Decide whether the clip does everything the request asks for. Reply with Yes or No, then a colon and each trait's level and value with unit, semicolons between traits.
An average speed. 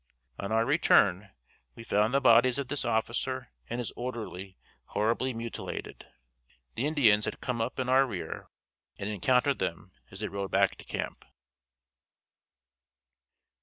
Yes: average, 145 wpm